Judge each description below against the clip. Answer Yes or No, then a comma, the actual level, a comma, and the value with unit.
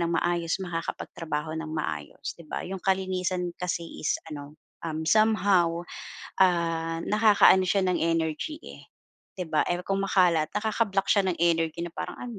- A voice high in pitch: No, medium, 175 Hz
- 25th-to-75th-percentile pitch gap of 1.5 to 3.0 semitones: Yes, average, 2.7 semitones